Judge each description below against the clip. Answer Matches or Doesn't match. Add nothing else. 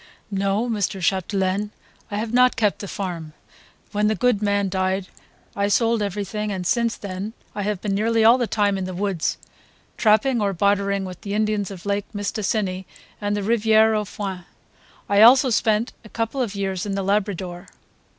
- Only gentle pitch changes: Matches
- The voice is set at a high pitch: Matches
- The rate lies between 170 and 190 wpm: Matches